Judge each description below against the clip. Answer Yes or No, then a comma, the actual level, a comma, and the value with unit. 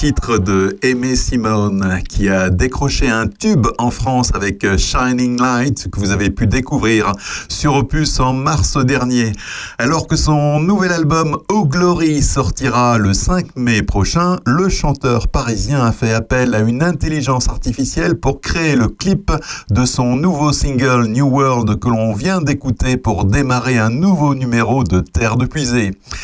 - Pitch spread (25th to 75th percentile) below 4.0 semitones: No, average, 4.6 semitones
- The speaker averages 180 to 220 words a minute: No, average, 160 wpm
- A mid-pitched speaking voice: No, low, 125 Hz